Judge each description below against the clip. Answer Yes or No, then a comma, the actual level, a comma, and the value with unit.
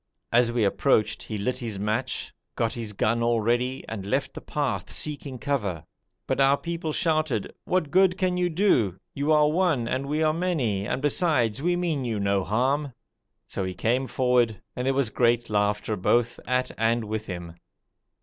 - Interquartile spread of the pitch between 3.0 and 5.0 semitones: No, wide, 5.4 semitones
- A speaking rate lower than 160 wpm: No, average, 180 wpm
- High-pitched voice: No, low, 125 Hz